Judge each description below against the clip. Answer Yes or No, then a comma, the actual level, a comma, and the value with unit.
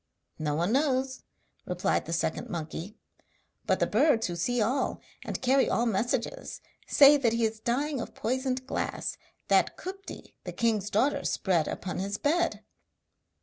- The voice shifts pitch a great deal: Yes, wide, 5.8 semitones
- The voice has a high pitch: Yes, high, 235 Hz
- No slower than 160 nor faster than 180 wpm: No, average, 150 wpm